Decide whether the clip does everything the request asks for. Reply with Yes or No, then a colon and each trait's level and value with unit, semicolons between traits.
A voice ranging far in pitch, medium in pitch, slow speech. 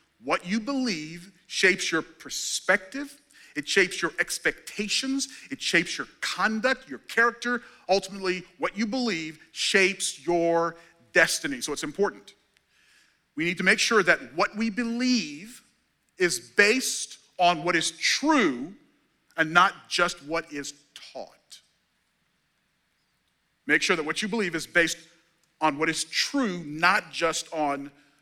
Yes: wide, 5.7 semitones; medium, 180 Hz; slow, 130 wpm